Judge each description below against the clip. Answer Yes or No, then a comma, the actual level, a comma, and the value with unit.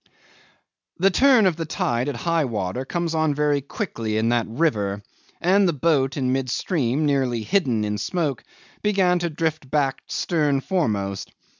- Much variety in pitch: Yes, wide, 6.0 semitones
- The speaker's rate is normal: Yes, average, 160 wpm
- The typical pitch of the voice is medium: Yes, medium, 145 Hz